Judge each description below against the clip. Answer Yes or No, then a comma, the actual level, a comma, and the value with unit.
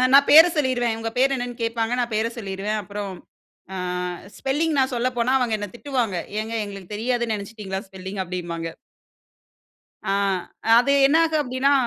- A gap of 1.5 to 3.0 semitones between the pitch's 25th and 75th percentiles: No, average, 4.4 semitones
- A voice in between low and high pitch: No, high, 230 Hz